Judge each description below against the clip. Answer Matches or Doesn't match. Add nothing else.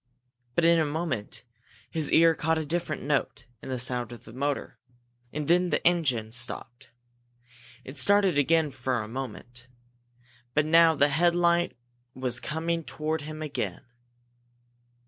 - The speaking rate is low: Doesn't match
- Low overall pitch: Doesn't match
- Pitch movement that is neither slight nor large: Matches